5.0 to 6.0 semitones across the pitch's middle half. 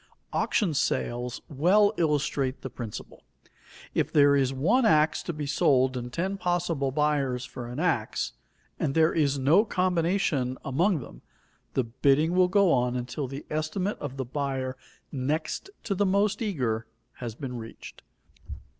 Yes: wide, 5.4 semitones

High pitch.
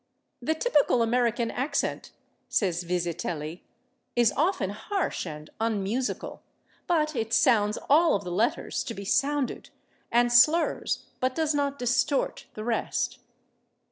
Yes: high, 240 Hz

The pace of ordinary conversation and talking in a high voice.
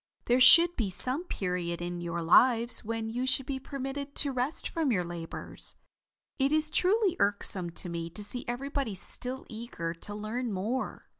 Yes: average, 170 wpm; high, 240 Hz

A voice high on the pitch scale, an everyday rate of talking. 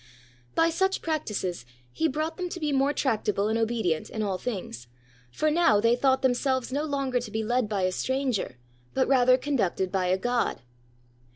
Yes: high, 245 Hz; average, 185 wpm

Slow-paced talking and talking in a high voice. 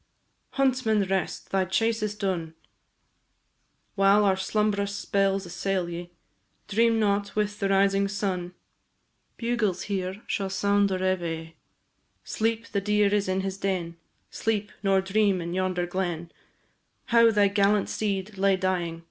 Yes: slow, 130 wpm; high, 195 Hz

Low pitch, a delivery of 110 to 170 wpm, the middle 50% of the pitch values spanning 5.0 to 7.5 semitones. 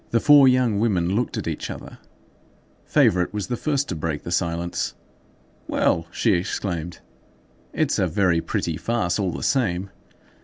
Yes: very low, 95 Hz; average, 155 wpm; average, 5.3 semitones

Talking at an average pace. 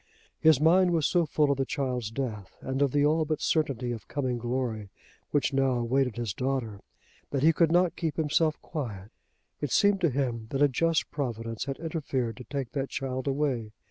Yes: average, 195 wpm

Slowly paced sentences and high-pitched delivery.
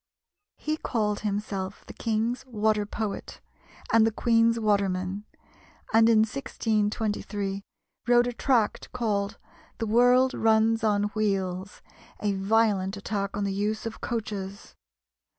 Yes: slow, 120 wpm; high, 215 Hz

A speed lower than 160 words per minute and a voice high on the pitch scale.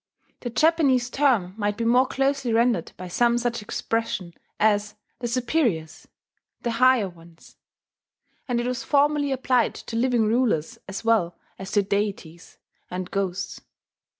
Yes: average, 140 wpm; high, 230 Hz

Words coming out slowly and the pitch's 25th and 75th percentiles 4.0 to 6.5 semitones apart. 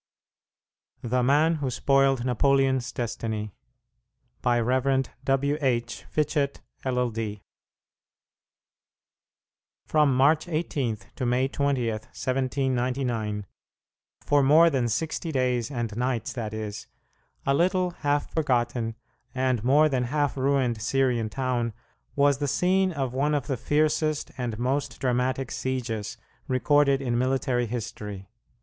No: slow, 115 wpm; average, 2.9 semitones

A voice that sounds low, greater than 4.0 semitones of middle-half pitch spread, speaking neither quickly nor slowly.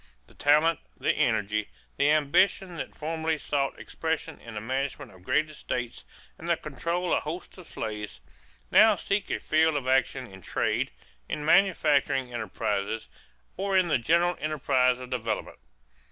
No: medium, 145 Hz; average, 5.0 semitones; average, 155 wpm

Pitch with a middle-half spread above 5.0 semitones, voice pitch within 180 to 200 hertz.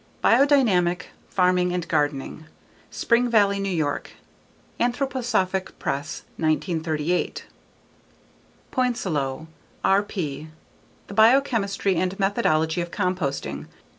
Yes: wide, 5.6 semitones; medium, 185 Hz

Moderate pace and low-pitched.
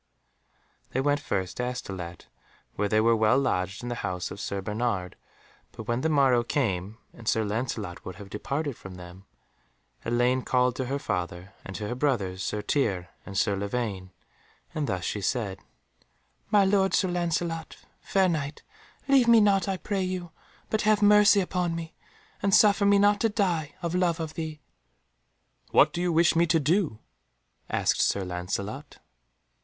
Yes: average, 170 wpm; low, 130 Hz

